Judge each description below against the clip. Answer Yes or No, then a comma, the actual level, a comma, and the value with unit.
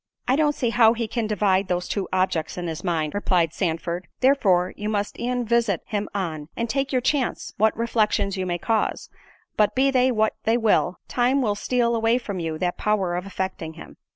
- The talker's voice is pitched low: No, high, 210 Hz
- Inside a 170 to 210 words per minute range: Yes, average, 200 wpm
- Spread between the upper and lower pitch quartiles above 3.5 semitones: Yes, average, 4.8 semitones